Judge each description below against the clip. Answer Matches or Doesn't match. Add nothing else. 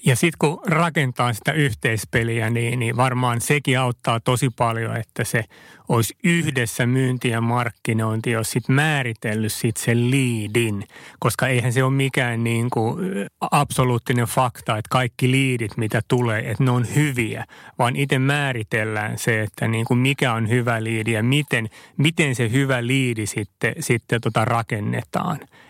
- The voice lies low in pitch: Matches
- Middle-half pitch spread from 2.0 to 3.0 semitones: Matches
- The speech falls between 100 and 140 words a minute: Doesn't match